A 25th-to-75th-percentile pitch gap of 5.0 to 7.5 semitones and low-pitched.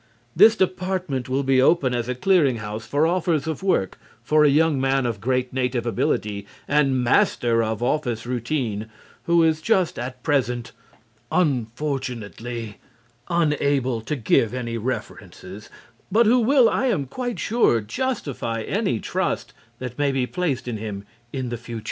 Yes: average, 5.3 semitones; low, 130 Hz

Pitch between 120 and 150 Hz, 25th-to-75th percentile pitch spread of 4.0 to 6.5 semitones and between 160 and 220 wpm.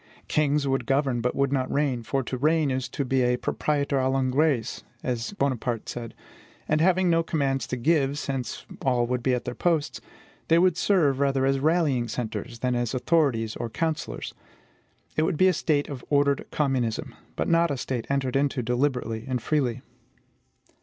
No: low, 135 Hz; average, 3.2 semitones; average, 180 wpm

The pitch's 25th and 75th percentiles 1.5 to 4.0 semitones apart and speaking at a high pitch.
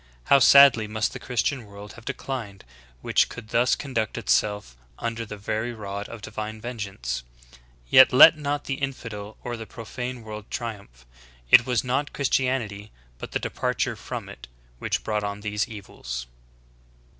No: average, 3.4 semitones; low, 110 Hz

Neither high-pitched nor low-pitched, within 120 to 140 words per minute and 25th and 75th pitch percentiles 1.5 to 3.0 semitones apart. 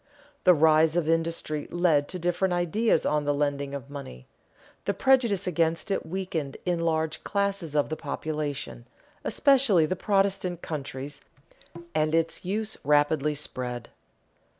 No: medium, 160 Hz; slow, 135 wpm; average, 3.8 semitones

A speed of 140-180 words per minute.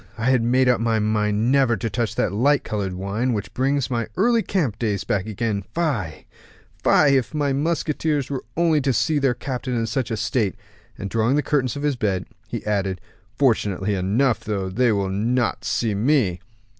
No: average, 195 wpm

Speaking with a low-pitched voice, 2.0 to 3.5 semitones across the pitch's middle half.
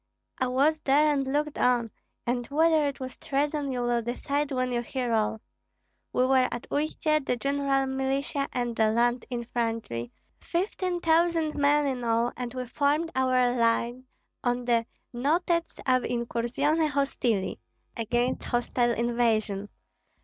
No: very high, 255 Hz; average, 3.2 semitones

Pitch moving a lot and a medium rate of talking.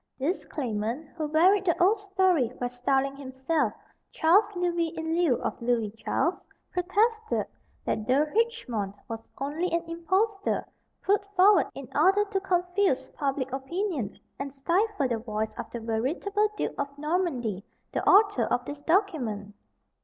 Yes: wide, 7.0 semitones; average, 145 wpm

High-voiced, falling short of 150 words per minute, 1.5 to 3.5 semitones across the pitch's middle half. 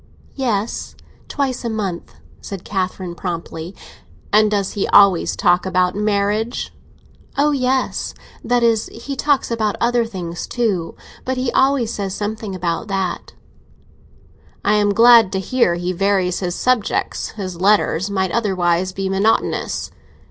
No: high, 205 Hz; slow, 135 wpm; average, 3.9 semitones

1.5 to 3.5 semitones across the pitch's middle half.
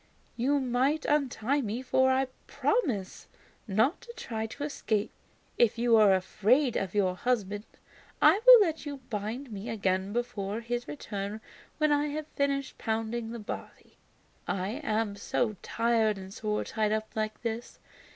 No: average, 4.5 semitones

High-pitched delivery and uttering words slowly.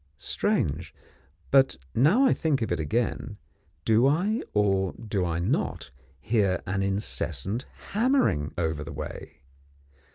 No: low, 105 Hz; slow, 125 wpm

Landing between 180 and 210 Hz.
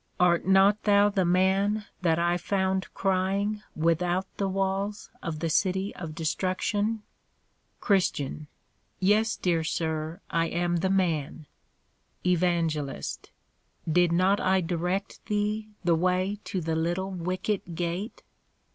Yes: medium, 185 Hz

